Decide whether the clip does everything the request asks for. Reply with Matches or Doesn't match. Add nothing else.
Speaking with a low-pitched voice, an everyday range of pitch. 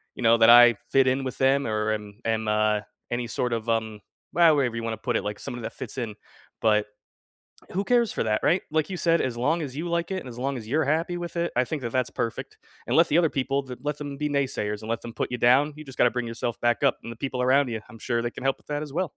Matches